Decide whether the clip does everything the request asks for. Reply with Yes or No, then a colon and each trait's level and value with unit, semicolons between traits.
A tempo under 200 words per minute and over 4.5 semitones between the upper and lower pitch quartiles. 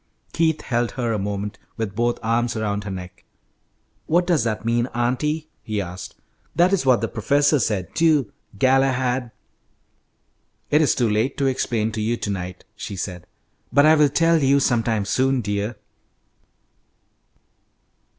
Yes: average, 150 wpm; average, 4.9 semitones